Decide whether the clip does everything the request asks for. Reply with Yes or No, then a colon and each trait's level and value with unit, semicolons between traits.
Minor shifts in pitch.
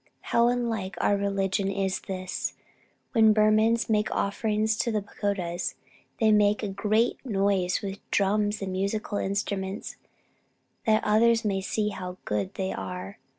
Yes: narrow, 2.0 semitones